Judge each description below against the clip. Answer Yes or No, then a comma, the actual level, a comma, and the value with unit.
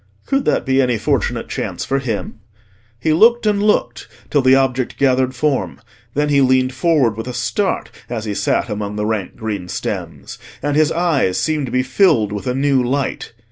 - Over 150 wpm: Yes, average, 190 wpm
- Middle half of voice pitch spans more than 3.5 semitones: Yes, average, 4.1 semitones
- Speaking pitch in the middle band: No, low, 130 Hz